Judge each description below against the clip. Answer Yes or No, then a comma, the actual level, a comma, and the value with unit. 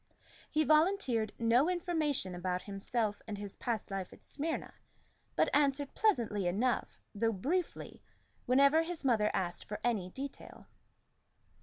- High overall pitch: Yes, high, 240 Hz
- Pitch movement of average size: No, wide, 6.8 semitones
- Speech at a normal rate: No, slow, 130 wpm